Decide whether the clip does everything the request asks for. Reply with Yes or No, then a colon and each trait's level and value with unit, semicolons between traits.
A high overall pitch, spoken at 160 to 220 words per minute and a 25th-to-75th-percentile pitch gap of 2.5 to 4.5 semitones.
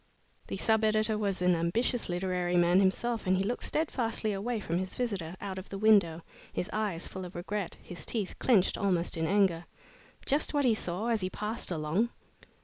Yes: high, 195 Hz; average, 190 wpm; average, 3.6 semitones